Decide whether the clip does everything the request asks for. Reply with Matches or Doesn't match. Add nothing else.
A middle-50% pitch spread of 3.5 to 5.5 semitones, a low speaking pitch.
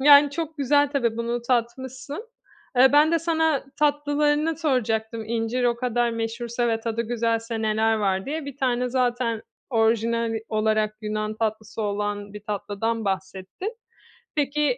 Doesn't match